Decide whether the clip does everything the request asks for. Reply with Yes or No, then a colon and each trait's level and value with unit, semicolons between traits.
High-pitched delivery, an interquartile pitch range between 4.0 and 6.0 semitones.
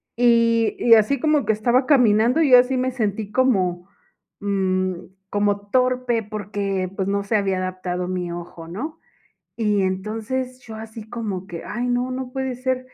Yes: high, 220 Hz; average, 4.5 semitones